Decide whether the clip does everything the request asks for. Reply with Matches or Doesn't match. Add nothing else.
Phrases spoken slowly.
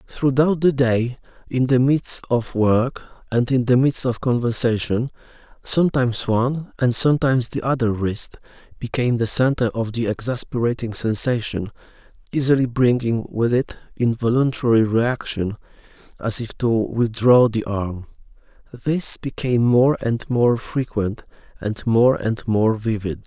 Matches